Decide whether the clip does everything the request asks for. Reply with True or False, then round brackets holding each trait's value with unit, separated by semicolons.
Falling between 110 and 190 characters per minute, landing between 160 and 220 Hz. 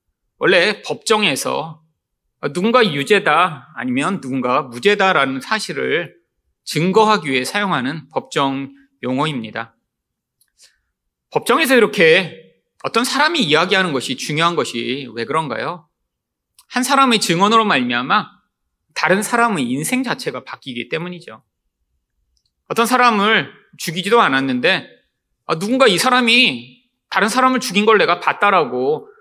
False (280 characters per minute; 190 Hz)